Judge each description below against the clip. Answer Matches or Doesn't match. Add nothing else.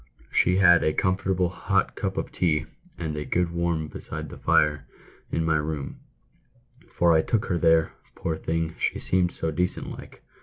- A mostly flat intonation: Matches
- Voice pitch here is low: Matches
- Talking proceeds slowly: Doesn't match